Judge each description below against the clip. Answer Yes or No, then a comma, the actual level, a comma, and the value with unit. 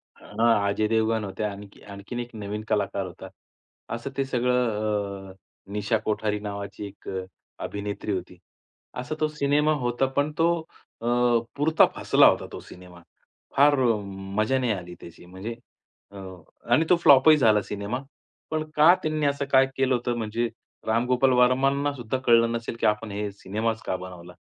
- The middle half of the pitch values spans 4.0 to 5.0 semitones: Yes, average, 4.6 semitones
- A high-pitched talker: No, low, 115 Hz